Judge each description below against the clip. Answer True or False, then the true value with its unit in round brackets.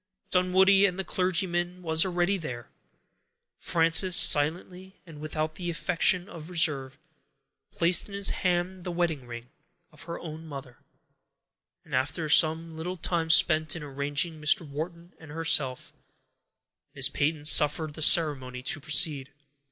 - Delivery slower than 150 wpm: True (135 wpm)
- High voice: False (160 Hz)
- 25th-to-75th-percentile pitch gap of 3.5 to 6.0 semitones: False (3.1 semitones)